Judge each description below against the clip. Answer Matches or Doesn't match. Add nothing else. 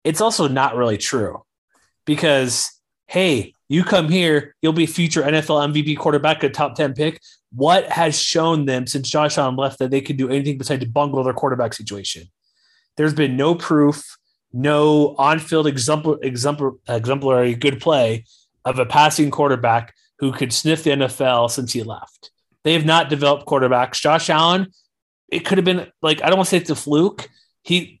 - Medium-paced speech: Matches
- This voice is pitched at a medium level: Matches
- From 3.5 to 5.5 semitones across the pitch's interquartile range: Doesn't match